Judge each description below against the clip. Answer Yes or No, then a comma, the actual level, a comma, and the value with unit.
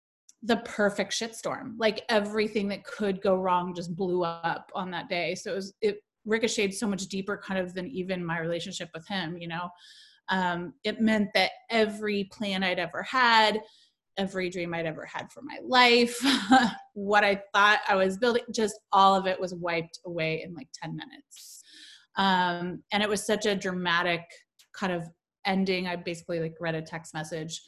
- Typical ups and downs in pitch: Yes, average, 3.5 semitones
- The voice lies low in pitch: No, high, 195 Hz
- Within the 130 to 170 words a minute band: No, average, 180 wpm